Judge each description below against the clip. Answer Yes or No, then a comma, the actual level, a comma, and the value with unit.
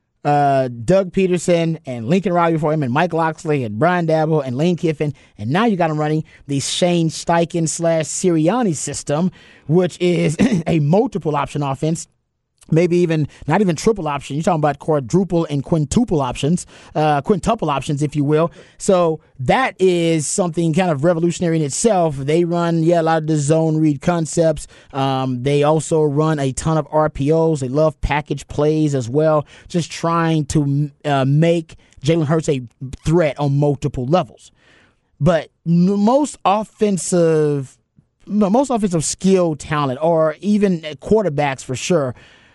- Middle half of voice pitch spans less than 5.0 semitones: Yes, average, 3.1 semitones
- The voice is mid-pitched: Yes, medium, 160 Hz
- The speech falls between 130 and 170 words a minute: Yes, average, 160 wpm